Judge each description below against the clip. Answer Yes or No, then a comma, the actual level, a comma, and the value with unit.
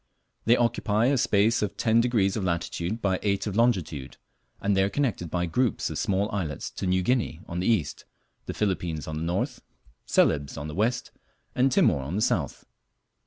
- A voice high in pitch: No, low, 100 Hz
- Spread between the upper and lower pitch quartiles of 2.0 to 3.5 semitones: No, average, 5.1 semitones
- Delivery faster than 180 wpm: Yes, average, 190 wpm